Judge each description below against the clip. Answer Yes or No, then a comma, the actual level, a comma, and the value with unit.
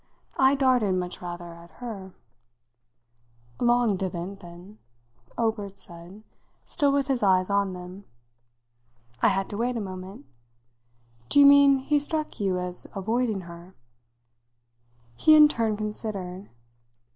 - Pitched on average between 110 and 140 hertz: No, high, 200 Hz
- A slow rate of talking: Yes, slow, 125 wpm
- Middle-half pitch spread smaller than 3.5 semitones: No, average, 4.9 semitones